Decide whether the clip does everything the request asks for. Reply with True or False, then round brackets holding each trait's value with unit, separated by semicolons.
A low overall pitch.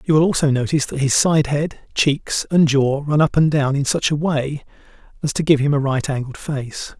False (145 Hz)